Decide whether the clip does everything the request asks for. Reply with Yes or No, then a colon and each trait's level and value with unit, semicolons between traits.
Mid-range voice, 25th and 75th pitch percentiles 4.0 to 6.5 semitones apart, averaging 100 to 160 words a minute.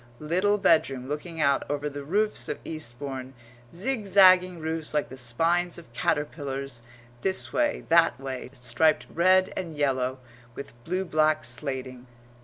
Yes: medium, 150 Hz; average, 4.8 semitones; slow, 135 wpm